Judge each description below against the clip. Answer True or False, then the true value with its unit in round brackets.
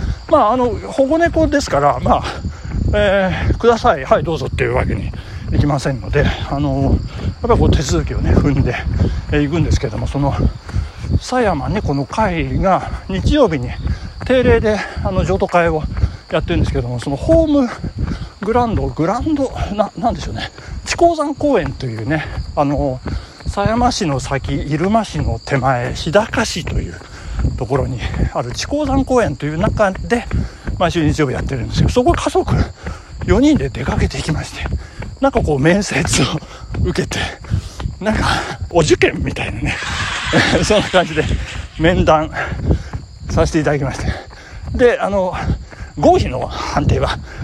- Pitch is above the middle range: False (165 Hz)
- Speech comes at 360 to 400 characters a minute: False (300 characters per minute)